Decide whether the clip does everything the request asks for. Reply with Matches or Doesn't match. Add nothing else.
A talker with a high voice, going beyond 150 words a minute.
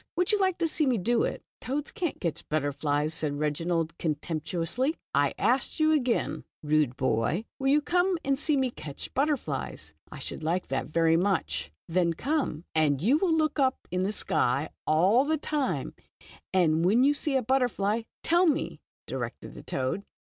Matches